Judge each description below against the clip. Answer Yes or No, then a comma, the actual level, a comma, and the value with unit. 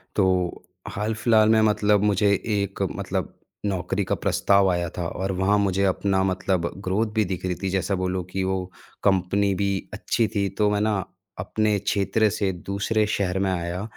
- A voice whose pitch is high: No, low, 100 Hz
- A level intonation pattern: Yes, narrow, 1.9 semitones